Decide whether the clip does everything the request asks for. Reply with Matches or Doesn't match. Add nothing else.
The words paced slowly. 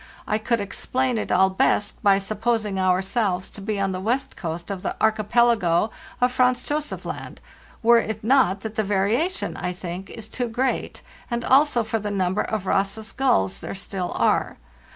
Doesn't match